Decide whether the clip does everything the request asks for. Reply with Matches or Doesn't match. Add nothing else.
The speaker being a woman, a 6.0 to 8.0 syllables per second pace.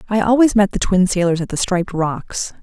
Doesn't match